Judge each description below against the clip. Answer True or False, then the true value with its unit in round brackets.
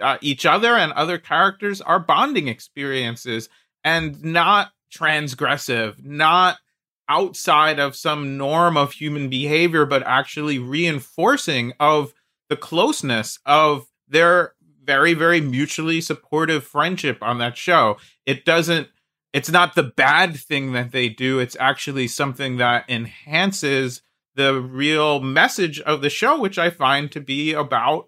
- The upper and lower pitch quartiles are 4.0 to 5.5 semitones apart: False (3.5 semitones)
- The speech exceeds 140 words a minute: False (135 wpm)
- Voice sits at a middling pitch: True (150 Hz)